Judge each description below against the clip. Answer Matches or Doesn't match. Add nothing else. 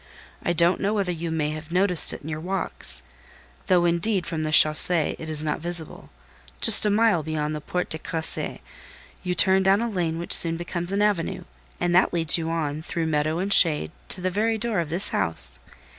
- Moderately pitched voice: Matches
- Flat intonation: Doesn't match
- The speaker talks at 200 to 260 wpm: Matches